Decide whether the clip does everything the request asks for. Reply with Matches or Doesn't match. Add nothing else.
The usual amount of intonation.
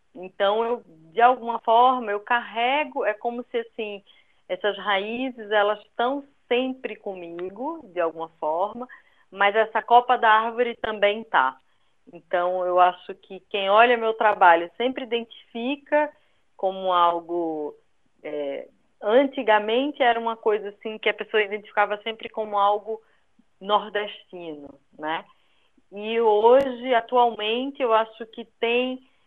Matches